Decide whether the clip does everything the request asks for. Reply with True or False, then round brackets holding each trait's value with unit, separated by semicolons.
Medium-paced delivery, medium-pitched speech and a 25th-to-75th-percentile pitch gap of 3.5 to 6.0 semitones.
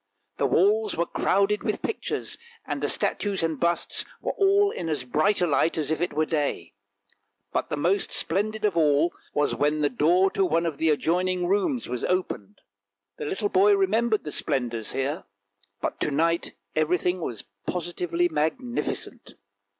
True (170 wpm; 170 Hz; 4.6 semitones)